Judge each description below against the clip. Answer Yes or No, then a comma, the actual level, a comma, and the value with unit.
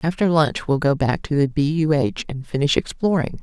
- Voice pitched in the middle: Yes, medium, 150 Hz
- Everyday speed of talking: No, fast, 230 wpm